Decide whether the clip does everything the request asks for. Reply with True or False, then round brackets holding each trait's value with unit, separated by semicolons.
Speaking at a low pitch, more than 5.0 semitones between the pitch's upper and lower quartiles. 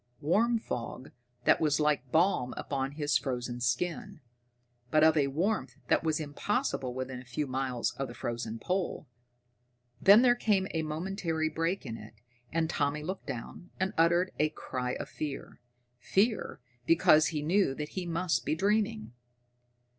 False (155 Hz; 5.5 semitones)